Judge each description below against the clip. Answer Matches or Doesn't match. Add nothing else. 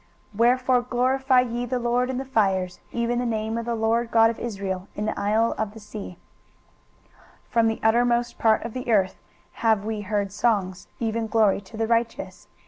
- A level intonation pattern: Matches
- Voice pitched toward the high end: Matches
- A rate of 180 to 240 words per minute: Matches